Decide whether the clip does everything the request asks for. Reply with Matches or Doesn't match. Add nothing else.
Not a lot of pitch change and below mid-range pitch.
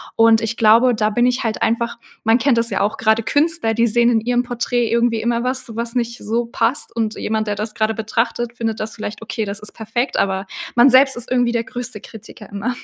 Doesn't match